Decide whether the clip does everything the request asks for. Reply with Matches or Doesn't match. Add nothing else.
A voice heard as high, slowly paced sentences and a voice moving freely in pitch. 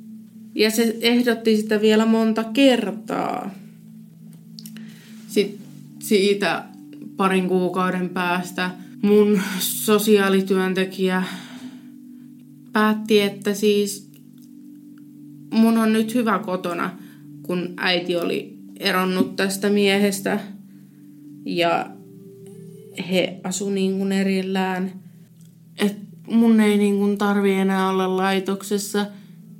Doesn't match